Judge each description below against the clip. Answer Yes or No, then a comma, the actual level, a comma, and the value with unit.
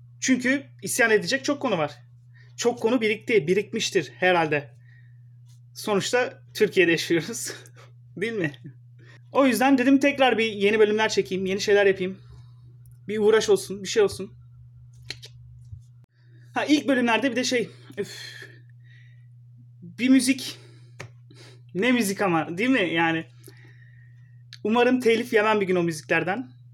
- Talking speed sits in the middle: Yes, average, 125 wpm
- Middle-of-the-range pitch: Yes, medium, 165 Hz